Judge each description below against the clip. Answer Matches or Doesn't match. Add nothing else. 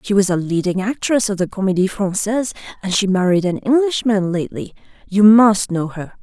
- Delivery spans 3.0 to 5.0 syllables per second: Doesn't match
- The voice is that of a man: Doesn't match